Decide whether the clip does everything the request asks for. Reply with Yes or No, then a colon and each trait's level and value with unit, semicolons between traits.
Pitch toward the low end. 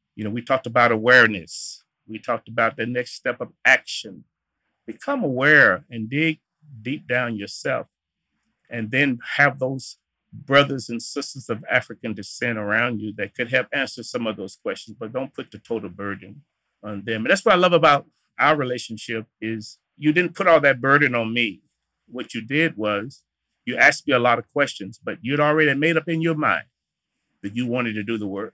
Yes: low, 125 Hz